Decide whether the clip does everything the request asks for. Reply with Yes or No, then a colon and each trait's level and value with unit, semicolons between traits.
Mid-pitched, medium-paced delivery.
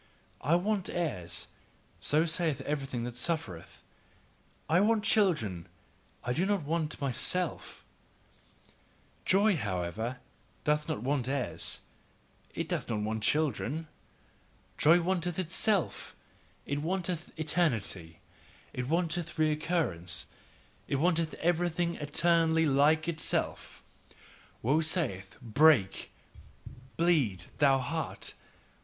No: medium, 155 Hz; slow, 100 wpm